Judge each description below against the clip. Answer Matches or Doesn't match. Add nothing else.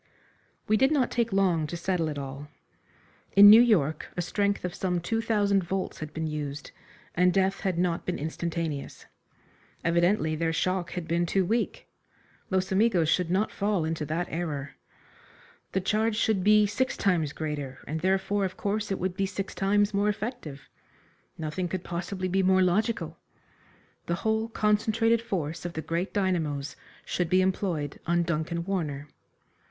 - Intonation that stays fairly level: Doesn't match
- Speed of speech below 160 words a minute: Doesn't match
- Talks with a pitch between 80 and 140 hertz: Doesn't match